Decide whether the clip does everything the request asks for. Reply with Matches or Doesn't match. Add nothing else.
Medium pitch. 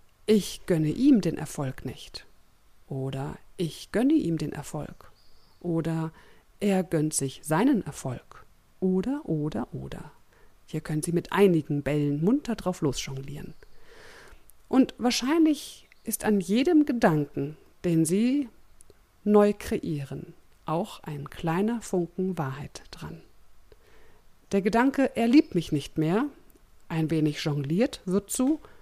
Matches